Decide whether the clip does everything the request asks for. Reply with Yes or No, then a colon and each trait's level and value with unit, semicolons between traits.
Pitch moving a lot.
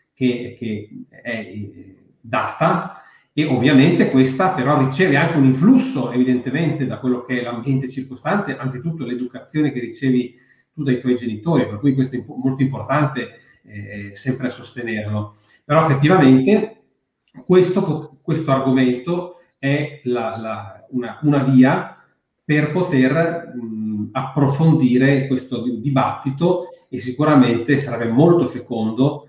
No: average, 3.3 semitones